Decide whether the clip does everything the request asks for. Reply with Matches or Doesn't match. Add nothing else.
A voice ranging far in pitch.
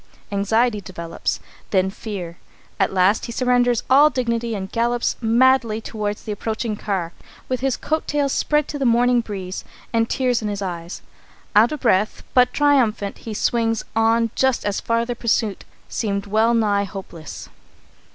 Doesn't match